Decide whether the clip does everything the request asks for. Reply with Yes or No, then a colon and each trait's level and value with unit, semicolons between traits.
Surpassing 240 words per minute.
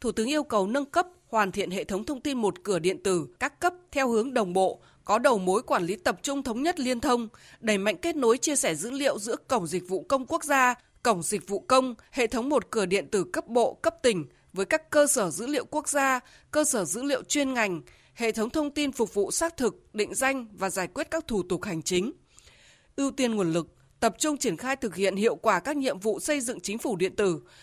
Yes: fast, 250 wpm